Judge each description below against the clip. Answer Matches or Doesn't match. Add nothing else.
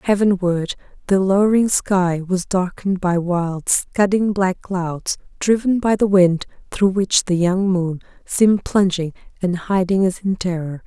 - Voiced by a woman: Matches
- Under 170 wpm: Matches